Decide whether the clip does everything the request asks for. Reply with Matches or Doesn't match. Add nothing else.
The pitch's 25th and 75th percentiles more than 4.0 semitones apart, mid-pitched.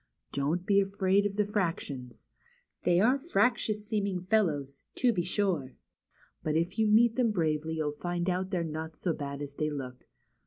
Matches